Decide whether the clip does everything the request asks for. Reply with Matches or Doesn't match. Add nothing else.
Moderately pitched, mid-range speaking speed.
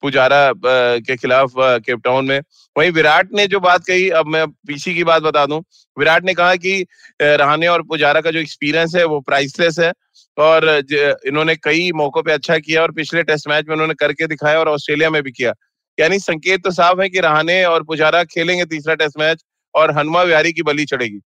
Doesn't match